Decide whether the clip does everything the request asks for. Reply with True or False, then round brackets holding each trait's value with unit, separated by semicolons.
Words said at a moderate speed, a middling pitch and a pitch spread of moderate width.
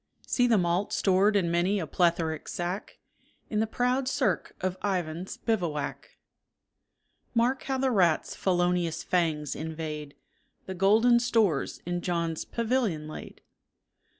False (125 wpm; 180 Hz; 4.9 semitones)